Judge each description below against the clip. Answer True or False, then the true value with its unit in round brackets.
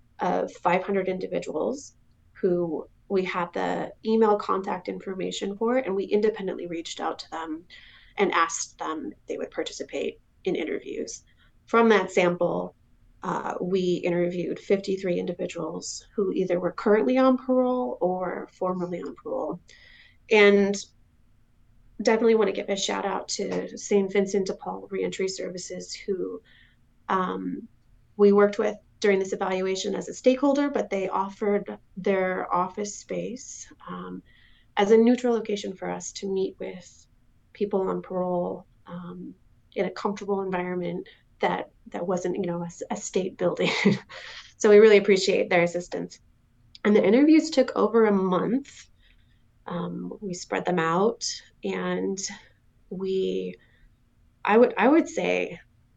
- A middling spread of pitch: True (3.7 semitones)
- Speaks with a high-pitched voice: True (195 Hz)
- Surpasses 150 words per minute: False (140 wpm)